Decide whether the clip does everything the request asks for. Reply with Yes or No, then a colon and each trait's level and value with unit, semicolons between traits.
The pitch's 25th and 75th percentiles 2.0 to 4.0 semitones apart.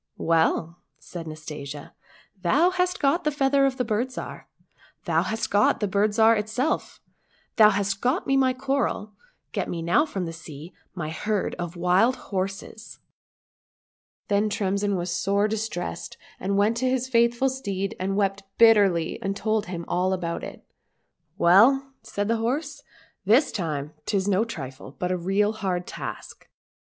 No: average, 4.8 semitones